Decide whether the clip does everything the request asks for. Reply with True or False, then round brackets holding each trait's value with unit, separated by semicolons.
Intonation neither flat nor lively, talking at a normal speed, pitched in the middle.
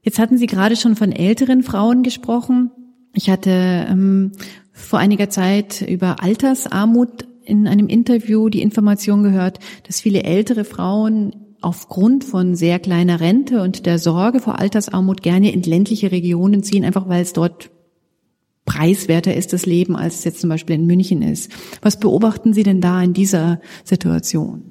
False (3.3 semitones; 160 wpm; 195 Hz)